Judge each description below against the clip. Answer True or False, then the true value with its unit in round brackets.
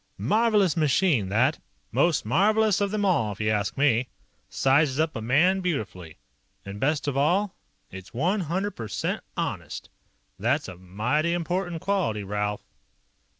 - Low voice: False (150 Hz)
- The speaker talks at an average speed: True (145 wpm)